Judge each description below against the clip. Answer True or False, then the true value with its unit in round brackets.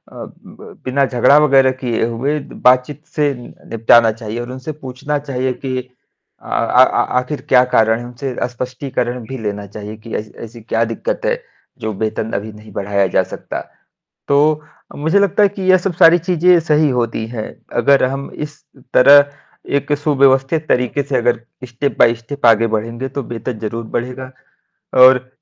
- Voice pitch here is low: True (130 Hz)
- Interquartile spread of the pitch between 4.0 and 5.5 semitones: False (3.6 semitones)